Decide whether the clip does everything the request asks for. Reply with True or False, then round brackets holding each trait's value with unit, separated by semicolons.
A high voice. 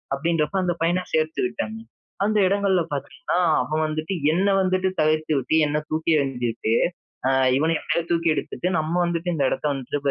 False (160 Hz)